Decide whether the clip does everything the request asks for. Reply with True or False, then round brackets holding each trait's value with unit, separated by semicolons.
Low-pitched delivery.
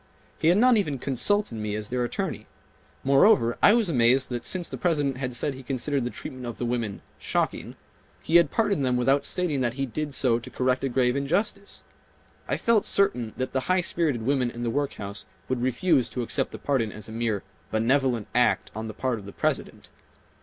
True (130 Hz)